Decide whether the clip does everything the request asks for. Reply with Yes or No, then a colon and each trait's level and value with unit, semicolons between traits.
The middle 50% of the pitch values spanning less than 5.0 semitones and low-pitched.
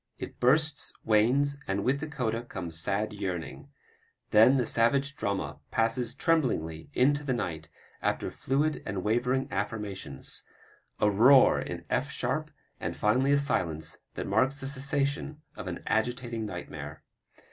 No: average, 5.3 semitones; low, 120 Hz